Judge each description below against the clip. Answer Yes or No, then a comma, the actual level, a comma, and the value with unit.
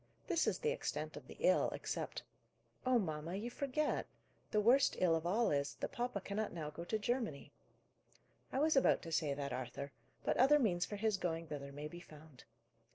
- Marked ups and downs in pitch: Yes, wide, 8.1 semitones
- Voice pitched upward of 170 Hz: Yes, medium, 185 Hz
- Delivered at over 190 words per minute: Yes, average, 200 wpm